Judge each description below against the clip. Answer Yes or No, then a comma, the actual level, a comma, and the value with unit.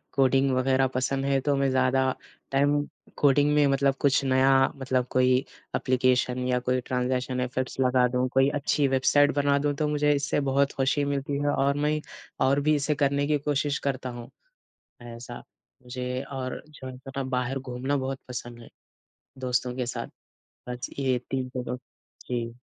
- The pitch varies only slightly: Yes, narrow, 1.7 semitones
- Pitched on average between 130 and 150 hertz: Yes, low, 135 Hz